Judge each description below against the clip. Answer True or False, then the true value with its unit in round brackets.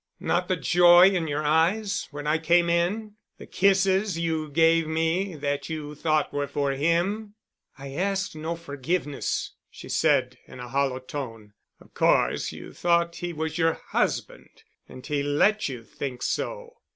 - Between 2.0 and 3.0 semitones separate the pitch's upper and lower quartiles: False (3.7 semitones)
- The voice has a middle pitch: True (160 Hz)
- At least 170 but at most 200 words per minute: False (160 wpm)